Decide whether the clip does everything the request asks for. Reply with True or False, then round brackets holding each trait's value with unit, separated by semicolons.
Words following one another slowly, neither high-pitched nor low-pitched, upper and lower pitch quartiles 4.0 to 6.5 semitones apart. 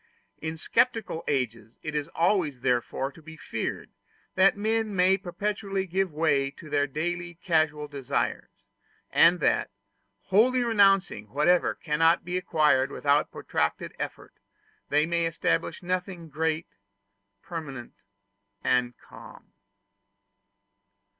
True (115 wpm; 165 Hz; 4.3 semitones)